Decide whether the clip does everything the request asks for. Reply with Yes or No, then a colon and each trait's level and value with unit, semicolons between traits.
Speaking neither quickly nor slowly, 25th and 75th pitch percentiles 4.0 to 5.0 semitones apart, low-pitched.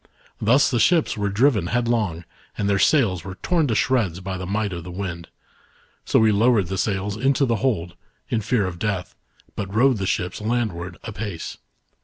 Yes: average, 185 wpm; average, 4.3 semitones; low, 105 Hz